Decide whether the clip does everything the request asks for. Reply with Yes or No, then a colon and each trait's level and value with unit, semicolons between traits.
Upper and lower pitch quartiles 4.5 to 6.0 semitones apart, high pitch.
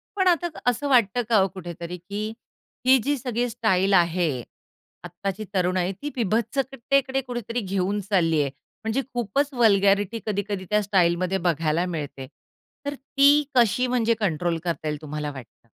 Yes: wide, 5.6 semitones; high, 200 Hz